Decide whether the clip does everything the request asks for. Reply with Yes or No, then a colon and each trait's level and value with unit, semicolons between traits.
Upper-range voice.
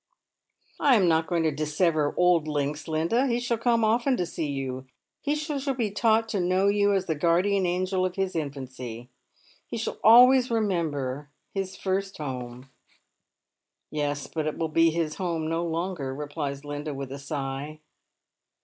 No: medium, 165 Hz